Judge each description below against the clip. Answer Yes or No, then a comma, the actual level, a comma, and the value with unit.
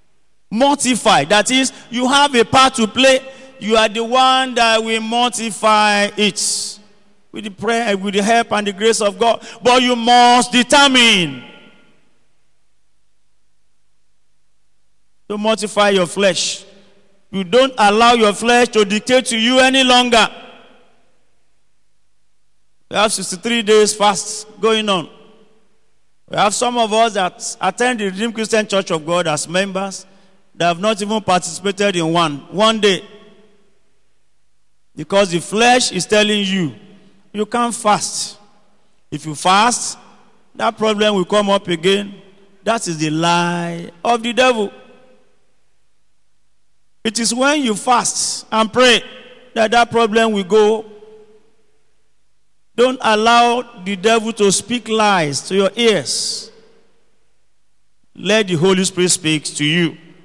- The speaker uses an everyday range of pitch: Yes, average, 3.0 semitones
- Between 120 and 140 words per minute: Yes, slow, 135 wpm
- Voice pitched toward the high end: Yes, high, 215 Hz